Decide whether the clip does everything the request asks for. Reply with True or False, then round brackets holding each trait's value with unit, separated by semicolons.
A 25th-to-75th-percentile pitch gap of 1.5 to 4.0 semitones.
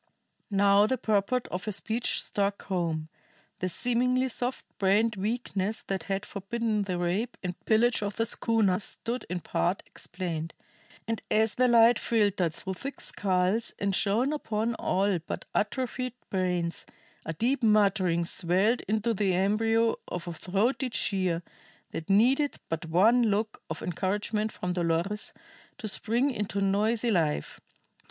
True (3.7 semitones)